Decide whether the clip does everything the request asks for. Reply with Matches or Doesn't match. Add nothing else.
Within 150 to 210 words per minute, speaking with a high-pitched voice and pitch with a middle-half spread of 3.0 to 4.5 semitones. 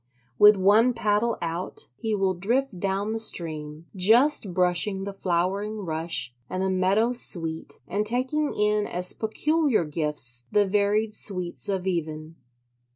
Doesn't match